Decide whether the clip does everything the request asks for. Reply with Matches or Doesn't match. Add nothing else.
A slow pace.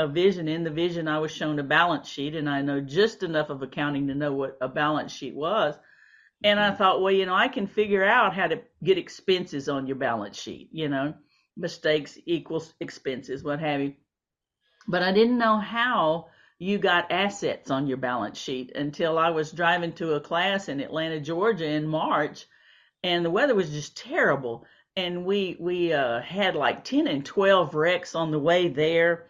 Doesn't match